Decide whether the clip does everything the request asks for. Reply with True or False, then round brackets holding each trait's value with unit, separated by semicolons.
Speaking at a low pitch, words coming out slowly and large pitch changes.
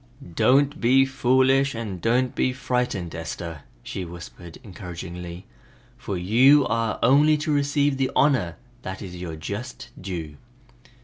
True (115 Hz; 130 wpm; 7.2 semitones)